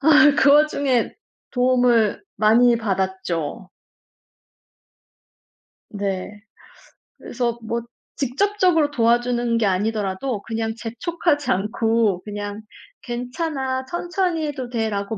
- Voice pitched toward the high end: Yes, high, 235 Hz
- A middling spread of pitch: Yes, average, 5.0 semitones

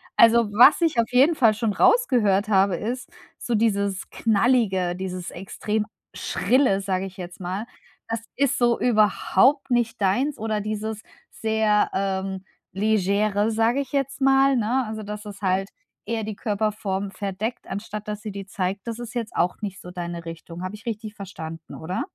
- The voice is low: No, high, 210 Hz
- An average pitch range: Yes, average, 3.2 semitones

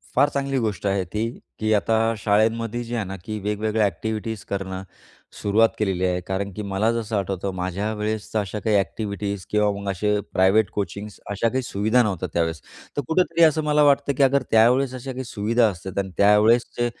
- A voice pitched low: Yes, low, 105 Hz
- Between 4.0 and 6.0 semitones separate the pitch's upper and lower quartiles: No, average, 2.8 semitones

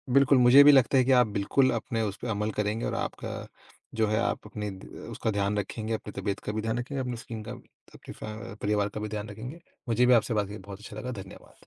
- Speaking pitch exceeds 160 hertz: No, low, 110 Hz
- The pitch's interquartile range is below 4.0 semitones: Yes, average, 2.8 semitones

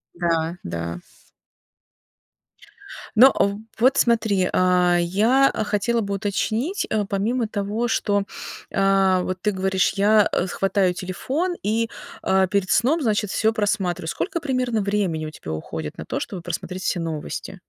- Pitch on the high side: Yes, high, 200 Hz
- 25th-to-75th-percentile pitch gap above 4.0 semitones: No, average, 3.6 semitones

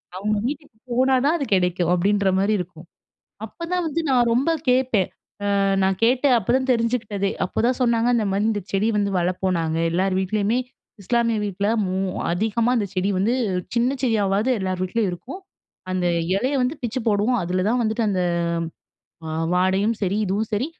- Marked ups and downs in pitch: No, average, 4.2 semitones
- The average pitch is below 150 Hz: No, high, 210 Hz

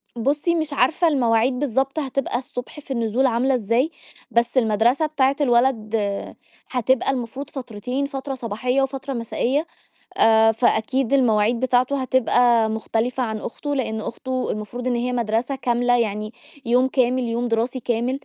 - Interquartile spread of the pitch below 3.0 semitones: Yes, narrow, 2.6 semitones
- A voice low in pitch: No, high, 245 Hz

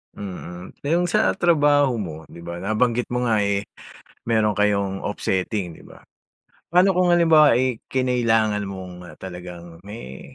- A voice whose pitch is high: No, low, 110 Hz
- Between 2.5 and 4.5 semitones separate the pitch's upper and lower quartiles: No, wide, 5.6 semitones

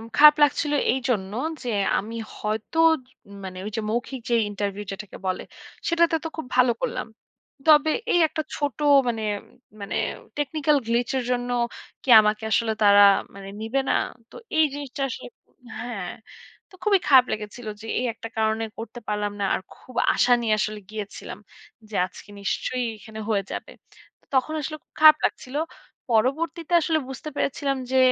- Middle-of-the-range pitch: No, high, 245 Hz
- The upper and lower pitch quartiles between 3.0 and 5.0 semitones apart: No, wide, 5.5 semitones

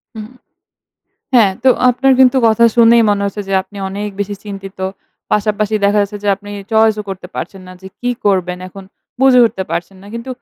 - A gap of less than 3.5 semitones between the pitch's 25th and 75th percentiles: Yes, narrow, 2.6 semitones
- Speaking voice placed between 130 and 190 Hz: No, high, 205 Hz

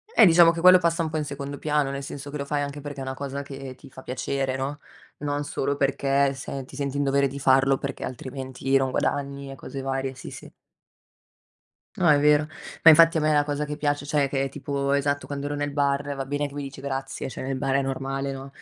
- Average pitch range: No, narrow, 1.2 semitones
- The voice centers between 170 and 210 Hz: No, medium, 140 Hz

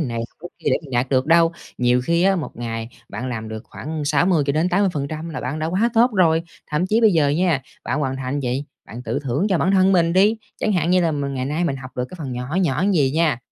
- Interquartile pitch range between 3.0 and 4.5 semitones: No, average, 5.1 semitones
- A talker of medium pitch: Yes, medium, 150 Hz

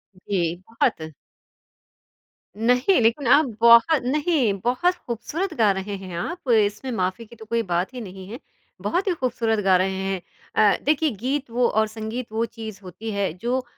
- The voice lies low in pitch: No, high, 230 Hz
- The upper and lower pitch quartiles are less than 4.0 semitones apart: No, average, 4.3 semitones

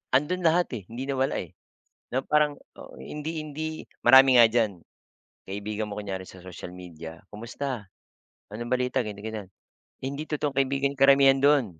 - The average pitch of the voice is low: Yes, low, 130 Hz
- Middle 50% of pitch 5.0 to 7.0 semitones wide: Yes, wide, 5.4 semitones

